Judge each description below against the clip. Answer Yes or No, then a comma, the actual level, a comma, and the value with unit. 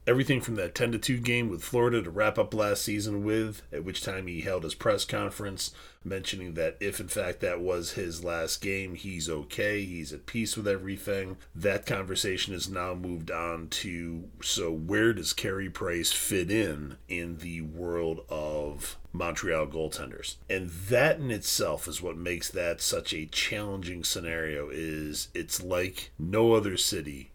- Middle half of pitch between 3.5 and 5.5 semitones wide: Yes, average, 4.0 semitones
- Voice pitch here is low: Yes, very low, 90 Hz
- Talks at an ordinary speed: Yes, average, 170 wpm